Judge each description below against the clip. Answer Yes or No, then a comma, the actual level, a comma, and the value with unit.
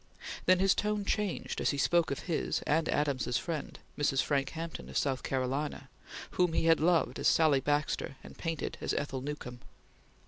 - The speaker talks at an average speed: Yes, average, 175 wpm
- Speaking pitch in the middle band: Yes, medium, 150 Hz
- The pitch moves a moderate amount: Yes, average, 3.3 semitones